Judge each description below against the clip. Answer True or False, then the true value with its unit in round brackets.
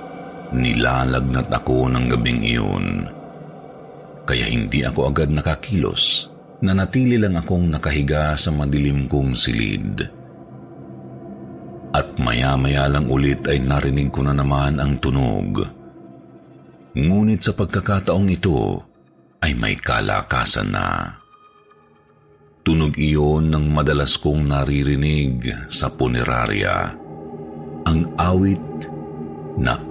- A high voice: False (75 Hz)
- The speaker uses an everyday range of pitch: True (3.1 semitones)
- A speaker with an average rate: False (100 wpm)